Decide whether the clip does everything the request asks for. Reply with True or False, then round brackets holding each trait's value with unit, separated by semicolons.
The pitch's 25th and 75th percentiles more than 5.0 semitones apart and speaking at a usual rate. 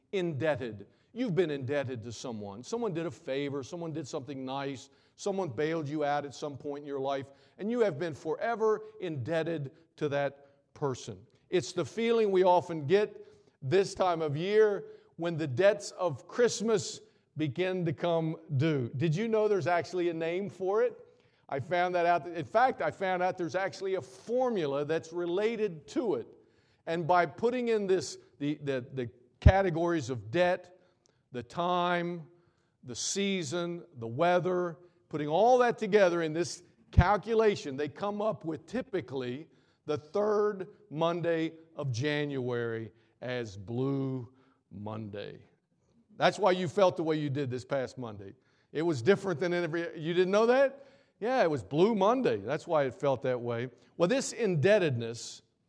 True (5.5 semitones; 160 wpm)